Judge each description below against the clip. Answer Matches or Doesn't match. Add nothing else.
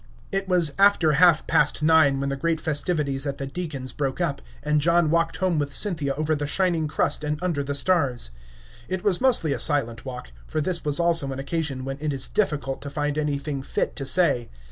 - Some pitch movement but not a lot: Matches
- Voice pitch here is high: Doesn't match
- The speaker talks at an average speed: Doesn't match